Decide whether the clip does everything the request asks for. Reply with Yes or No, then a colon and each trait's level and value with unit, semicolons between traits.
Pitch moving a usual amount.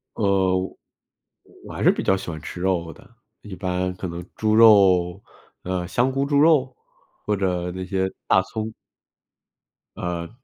Yes: average, 3.3 semitones